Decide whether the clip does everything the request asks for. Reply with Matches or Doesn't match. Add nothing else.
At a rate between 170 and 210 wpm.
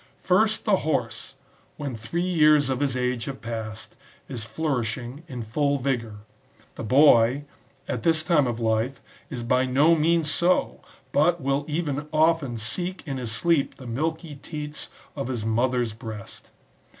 Doesn't match